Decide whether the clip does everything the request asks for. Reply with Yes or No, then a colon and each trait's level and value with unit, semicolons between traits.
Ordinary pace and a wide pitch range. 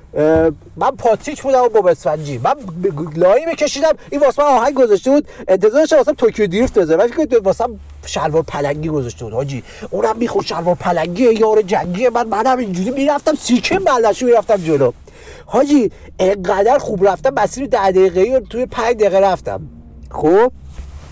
No: fast, 160 wpm; wide, 7.4 semitones